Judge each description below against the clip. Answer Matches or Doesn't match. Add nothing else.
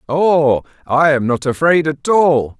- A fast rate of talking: Doesn't match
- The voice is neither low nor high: Matches